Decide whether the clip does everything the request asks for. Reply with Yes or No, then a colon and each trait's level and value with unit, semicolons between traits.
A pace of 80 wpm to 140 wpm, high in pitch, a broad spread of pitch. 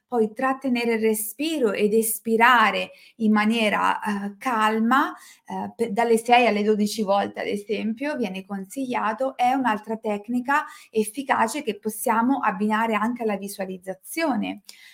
No: average, 120 wpm; high, 220 Hz; average, 2.7 semitones